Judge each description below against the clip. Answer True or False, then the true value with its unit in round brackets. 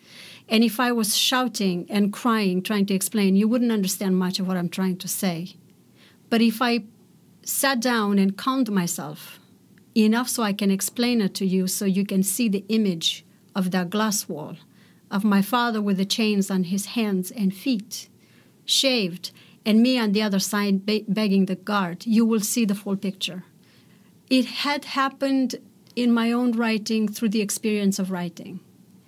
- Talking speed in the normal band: True (175 wpm)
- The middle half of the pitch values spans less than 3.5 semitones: True (3.1 semitones)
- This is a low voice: False (205 Hz)